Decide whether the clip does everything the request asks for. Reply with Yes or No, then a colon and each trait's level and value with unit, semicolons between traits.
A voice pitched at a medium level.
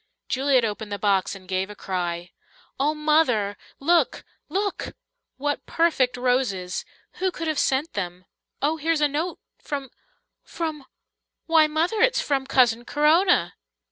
No: very high, 275 Hz